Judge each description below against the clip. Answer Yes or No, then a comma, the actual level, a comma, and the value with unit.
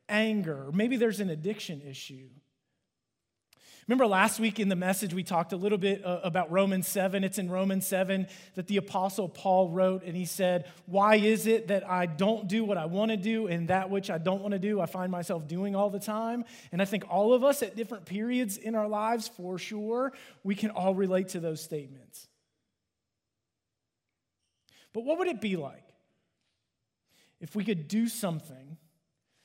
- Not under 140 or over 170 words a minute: No, average, 185 wpm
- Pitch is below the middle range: No, high, 190 Hz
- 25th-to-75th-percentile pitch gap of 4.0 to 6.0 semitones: Yes, average, 4.4 semitones